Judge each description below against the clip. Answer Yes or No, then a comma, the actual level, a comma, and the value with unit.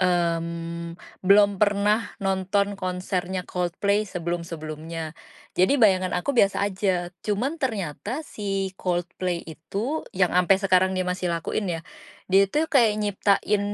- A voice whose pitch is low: No, medium, 185 Hz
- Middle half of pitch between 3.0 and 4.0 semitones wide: No, narrow, 2.6 semitones